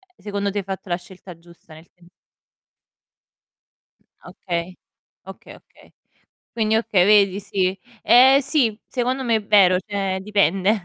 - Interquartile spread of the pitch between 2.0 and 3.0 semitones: Yes, average, 2.7 semitones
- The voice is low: No, high, 200 Hz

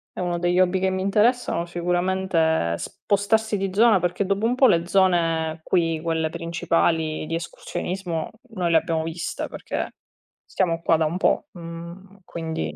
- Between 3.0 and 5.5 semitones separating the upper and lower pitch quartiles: No, narrow, 2.4 semitones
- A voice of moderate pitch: Yes, medium, 175 Hz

